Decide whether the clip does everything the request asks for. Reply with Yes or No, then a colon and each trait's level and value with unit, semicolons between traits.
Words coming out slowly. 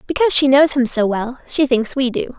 No: fast, 250 wpm